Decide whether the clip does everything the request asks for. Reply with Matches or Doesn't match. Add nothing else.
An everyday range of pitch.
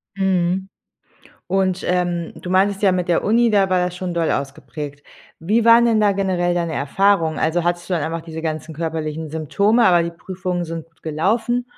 Matches